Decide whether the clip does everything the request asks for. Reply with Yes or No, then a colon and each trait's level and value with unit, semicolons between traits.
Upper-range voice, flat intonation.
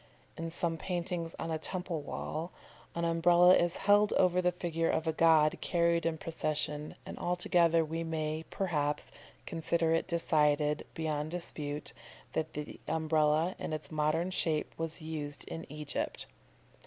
No: medium, 165 Hz; narrow, 1.8 semitones